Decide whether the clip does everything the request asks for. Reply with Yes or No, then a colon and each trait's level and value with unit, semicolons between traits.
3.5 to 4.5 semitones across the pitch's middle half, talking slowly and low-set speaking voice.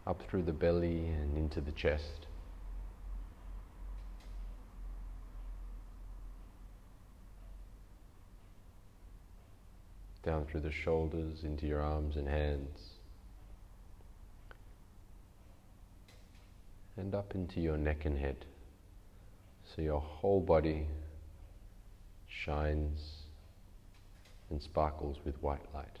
Yes: average, 3.9 semitones; slow, 80 wpm; very low, 90 Hz